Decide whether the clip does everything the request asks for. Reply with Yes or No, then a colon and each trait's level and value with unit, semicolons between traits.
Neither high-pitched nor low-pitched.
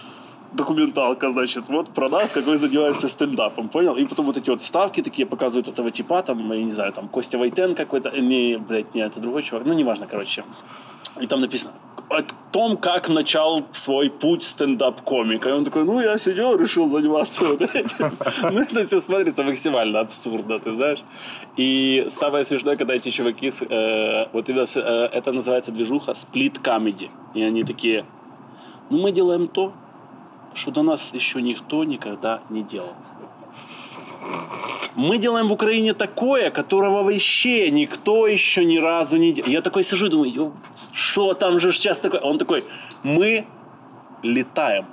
Yes: medium, 160 Hz